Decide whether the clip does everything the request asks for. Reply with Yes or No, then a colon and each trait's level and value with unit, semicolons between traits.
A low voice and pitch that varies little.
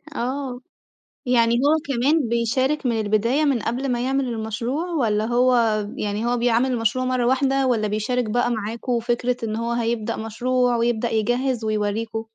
No: high, 240 Hz; narrow, 2.3 semitones